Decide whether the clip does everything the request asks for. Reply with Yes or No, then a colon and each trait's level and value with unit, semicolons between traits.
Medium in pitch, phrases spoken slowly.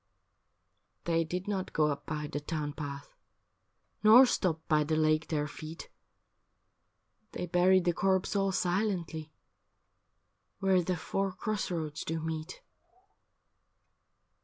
Yes: medium, 165 Hz; slow, 125 wpm